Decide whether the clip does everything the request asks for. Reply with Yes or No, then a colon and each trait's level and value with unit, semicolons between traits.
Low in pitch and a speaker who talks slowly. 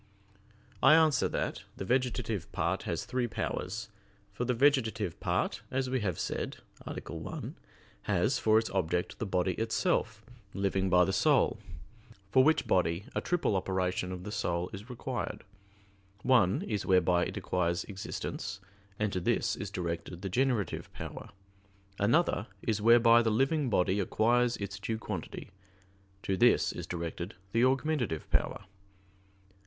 No: low, 105 Hz; average, 145 wpm